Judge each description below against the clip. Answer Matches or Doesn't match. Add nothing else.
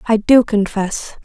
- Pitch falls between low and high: Doesn't match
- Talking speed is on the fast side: Doesn't match